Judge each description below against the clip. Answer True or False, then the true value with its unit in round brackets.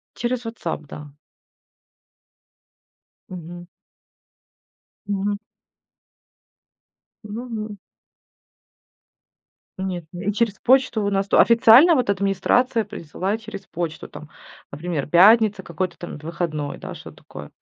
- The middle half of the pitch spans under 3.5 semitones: False (4.4 semitones)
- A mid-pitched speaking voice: False (200 Hz)